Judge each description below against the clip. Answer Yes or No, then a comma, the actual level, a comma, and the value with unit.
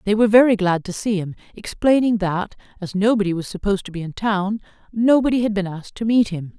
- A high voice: Yes, high, 205 Hz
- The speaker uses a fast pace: Yes, fast, 220 wpm